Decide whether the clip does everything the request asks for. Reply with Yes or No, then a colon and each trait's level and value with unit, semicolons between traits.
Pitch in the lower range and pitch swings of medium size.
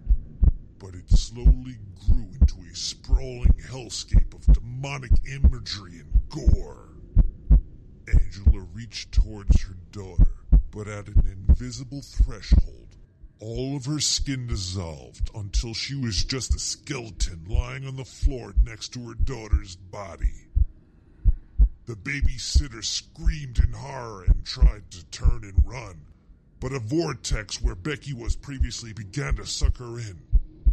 No: very low, 95 Hz; wide, 6.8 semitones